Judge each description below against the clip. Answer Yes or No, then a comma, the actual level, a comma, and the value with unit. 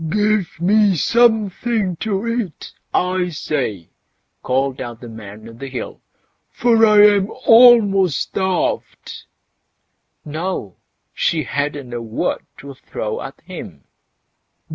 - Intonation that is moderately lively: No, wide, 8.0 semitones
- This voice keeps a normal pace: No, slow, 115 wpm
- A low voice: No, medium, 185 Hz